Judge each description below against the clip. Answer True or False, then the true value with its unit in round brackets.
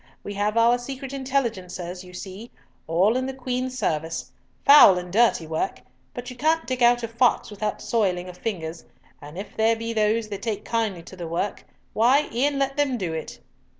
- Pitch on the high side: True (220 Hz)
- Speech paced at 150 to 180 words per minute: False (190 wpm)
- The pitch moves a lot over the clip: True (5.7 semitones)